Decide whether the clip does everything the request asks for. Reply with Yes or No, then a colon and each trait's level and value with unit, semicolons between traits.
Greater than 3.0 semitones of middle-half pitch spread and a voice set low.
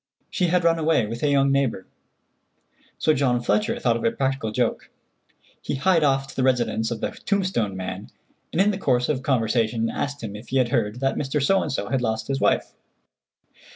Yes: average, 4.0 semitones; low, 130 Hz